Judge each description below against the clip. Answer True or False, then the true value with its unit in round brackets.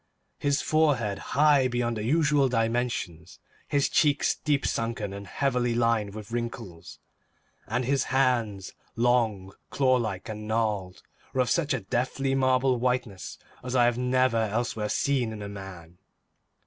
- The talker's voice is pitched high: False (120 Hz)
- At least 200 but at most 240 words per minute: False (145 wpm)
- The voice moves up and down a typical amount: True (3.5 semitones)